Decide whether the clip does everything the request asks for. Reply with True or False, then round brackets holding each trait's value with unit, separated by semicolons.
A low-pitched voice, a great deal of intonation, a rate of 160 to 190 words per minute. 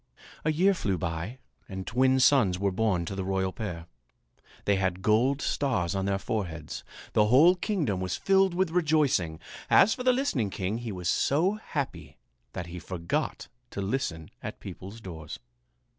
True (105 Hz; 7.5 semitones; 165 wpm)